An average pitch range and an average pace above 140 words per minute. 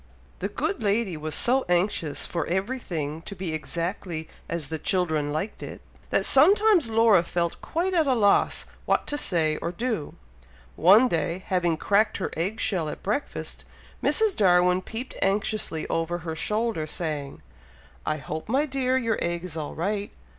No: wide, 5.7 semitones; average, 160 wpm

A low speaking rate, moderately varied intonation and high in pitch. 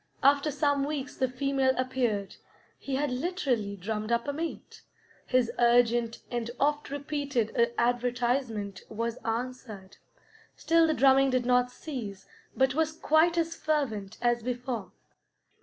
Yes: slow, 130 wpm; average, 3.3 semitones; very high, 255 Hz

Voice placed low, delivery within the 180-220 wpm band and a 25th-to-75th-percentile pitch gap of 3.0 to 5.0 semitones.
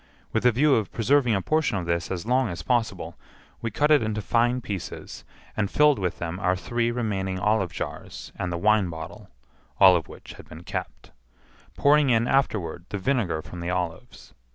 No: low, 105 Hz; average, 190 wpm; wide, 5.4 semitones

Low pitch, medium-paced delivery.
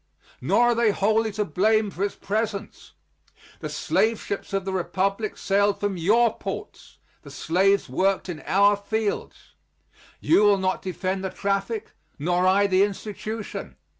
No: high, 200 Hz; average, 150 wpm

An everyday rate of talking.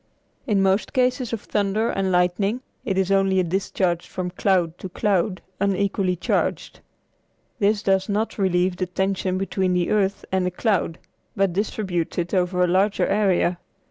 Yes: average, 160 wpm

